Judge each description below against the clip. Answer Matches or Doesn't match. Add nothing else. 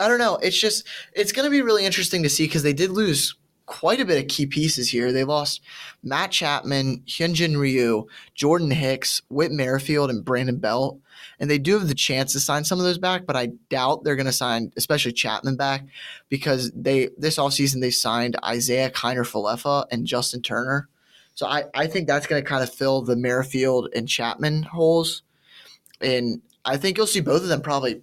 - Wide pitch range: Doesn't match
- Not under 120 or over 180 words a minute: Doesn't match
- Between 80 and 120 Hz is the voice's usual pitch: Doesn't match